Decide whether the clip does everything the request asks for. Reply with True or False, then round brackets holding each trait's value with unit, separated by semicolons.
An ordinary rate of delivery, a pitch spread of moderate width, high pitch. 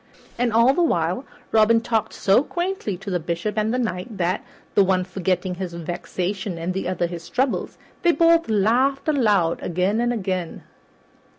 True (170 wpm; 4.9 semitones; 200 Hz)